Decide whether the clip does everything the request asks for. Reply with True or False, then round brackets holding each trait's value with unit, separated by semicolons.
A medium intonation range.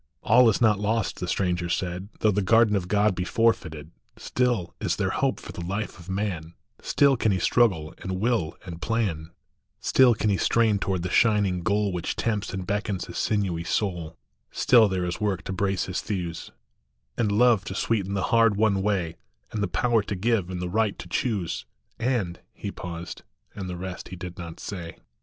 True (3.5 semitones)